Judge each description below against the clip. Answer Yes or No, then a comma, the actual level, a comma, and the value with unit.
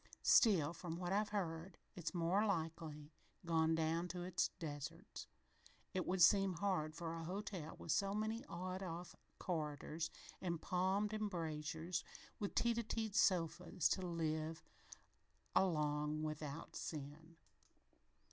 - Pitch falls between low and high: Yes, medium, 170 Hz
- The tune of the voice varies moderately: Yes, average, 3.1 semitones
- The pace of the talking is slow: Yes, slow, 130 wpm